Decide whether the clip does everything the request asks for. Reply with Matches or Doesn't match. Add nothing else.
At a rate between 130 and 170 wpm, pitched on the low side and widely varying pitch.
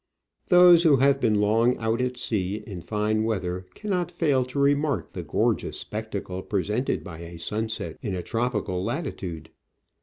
Matches